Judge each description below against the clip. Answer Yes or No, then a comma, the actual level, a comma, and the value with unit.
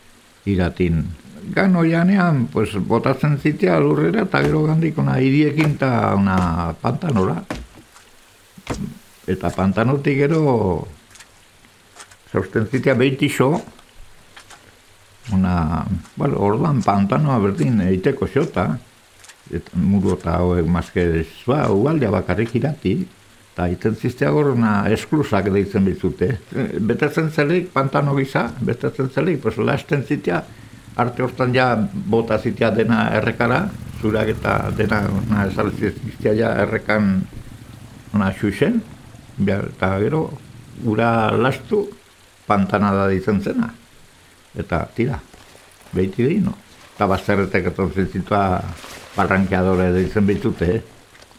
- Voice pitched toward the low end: Yes, low, 110 Hz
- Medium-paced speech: No, slow, 105 wpm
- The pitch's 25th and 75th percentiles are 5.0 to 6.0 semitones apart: Yes, wide, 5.5 semitones